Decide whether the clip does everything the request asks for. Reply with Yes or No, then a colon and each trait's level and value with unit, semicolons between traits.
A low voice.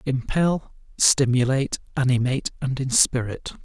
Yes: low, 130 Hz